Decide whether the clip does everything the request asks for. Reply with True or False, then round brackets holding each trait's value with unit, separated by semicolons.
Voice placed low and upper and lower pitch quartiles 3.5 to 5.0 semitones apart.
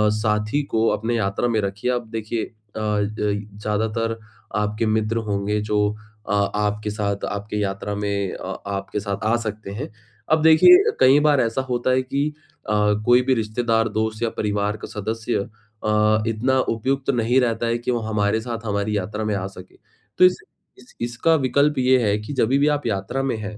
False (110 Hz; 2.7 semitones)